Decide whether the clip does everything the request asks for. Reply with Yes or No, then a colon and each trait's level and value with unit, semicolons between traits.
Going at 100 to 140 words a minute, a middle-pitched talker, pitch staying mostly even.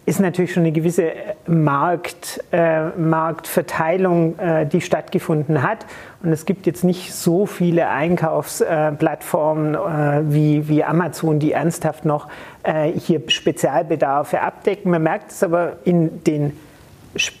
Yes: average, 130 wpm; medium, 165 Hz; narrow, 2.3 semitones